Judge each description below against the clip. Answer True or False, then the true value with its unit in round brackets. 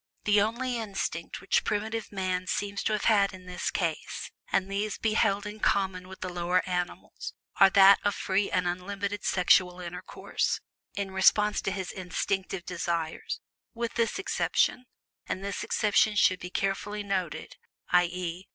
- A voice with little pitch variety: True (2.2 semitones)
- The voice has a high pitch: True (195 Hz)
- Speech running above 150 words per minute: True (160 wpm)